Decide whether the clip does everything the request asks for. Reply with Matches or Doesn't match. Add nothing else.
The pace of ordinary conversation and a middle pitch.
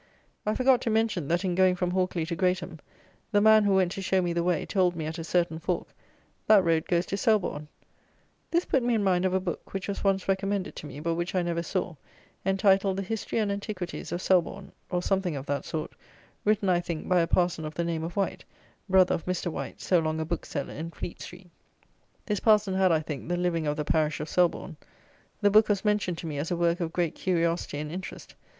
Doesn't match